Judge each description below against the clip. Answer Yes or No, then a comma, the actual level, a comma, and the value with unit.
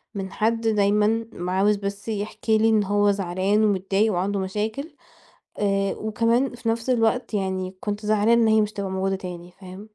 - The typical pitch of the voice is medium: No, high, 205 Hz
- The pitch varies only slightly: Yes, narrow, 2.2 semitones